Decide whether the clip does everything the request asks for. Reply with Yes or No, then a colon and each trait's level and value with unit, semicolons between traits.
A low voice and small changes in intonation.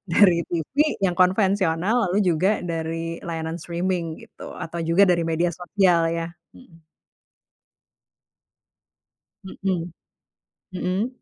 No: medium, 175 Hz; narrow, 2.3 semitones